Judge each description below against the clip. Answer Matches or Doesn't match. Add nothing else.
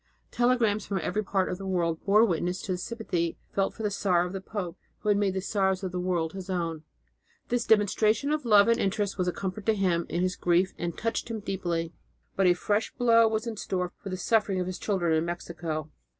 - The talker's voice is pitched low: Doesn't match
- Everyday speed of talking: Doesn't match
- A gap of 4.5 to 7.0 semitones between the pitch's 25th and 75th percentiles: Doesn't match